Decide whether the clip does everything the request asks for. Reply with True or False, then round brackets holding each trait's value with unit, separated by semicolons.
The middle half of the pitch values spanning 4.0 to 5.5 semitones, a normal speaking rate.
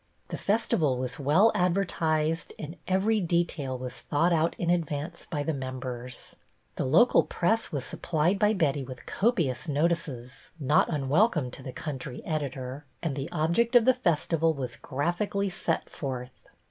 True (4.7 semitones; 160 wpm)